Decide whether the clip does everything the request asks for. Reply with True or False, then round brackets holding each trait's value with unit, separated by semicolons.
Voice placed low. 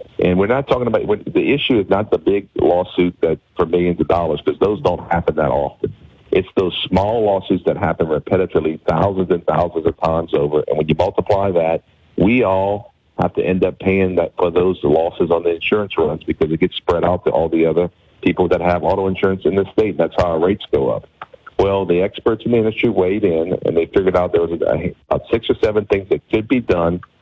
True (90 Hz)